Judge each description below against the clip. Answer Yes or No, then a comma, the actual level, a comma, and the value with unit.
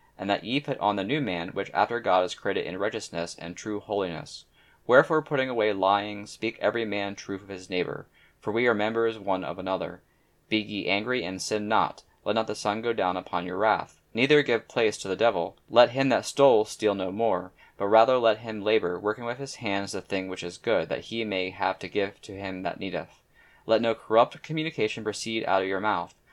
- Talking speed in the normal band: No, fast, 220 wpm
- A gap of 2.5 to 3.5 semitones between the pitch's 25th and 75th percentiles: Yes, average, 3.1 semitones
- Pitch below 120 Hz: Yes, low, 105 Hz